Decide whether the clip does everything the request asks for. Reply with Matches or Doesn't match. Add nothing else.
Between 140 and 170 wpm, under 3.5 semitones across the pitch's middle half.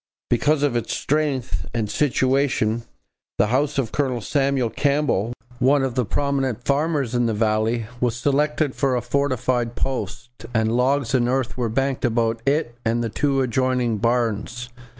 Matches